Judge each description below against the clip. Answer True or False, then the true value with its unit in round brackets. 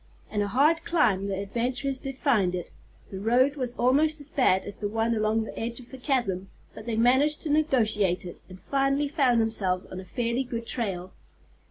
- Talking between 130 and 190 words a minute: False (200 wpm)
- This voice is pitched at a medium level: False (235 Hz)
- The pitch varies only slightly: False (5.1 semitones)